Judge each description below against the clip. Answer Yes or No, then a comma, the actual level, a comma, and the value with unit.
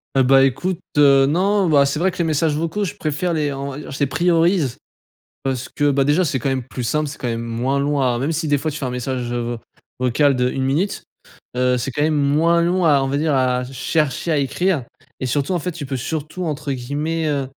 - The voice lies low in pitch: No, medium, 145 Hz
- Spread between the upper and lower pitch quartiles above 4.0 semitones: No, average, 3.4 semitones